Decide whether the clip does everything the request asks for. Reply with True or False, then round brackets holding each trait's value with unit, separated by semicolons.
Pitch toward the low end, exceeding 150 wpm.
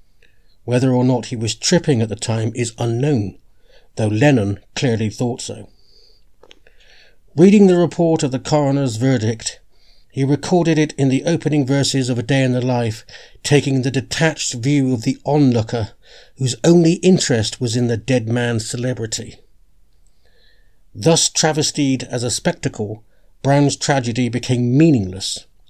False (130 Hz; 140 wpm)